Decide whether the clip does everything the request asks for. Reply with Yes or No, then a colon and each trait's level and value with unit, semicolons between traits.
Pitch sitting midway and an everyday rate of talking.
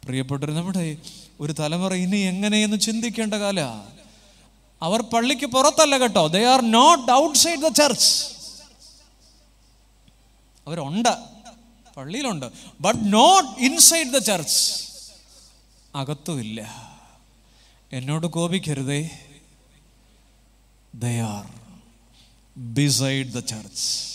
Yes: medium, 155 Hz; average, 80 wpm